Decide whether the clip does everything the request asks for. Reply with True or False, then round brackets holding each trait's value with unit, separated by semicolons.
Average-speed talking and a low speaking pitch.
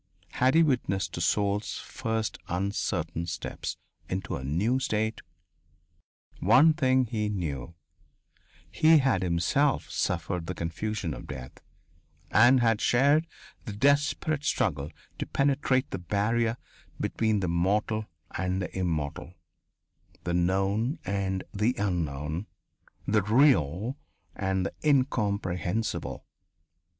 False (110 wpm; 105 Hz)